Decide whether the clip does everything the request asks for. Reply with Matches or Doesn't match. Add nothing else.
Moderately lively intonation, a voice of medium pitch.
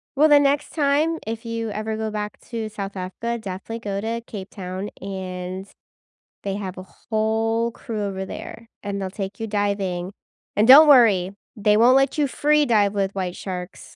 Doesn't match